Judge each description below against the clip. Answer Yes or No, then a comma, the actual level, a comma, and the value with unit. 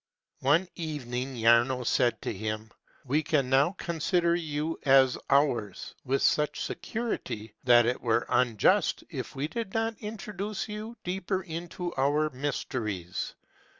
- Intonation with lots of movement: Yes, wide, 6.1 semitones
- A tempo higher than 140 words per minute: No, slow, 135 wpm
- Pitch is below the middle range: No, medium, 145 Hz